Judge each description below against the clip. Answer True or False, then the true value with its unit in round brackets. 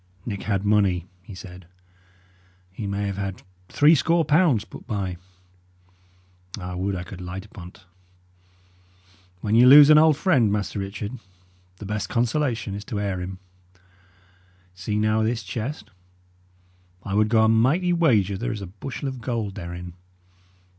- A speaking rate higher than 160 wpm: False (150 wpm)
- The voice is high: False (105 Hz)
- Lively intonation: False (4.2 semitones)